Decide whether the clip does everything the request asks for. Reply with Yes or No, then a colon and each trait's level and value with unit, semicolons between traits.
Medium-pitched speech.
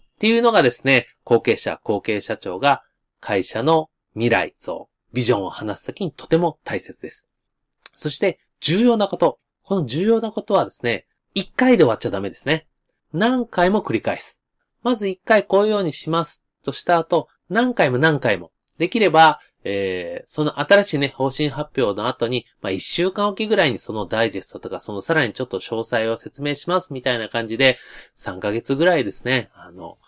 Yes: medium, 150 Hz